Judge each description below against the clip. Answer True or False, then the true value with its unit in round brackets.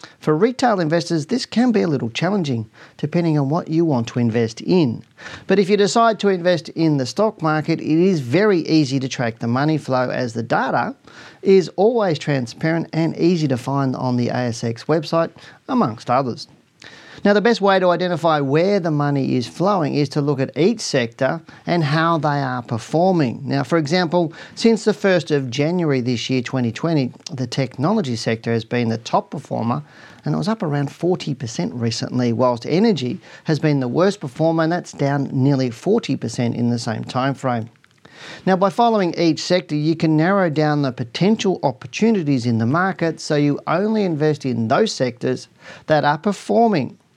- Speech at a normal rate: True (180 wpm)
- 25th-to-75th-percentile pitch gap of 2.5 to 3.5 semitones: False (5.6 semitones)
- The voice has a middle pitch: True (155 Hz)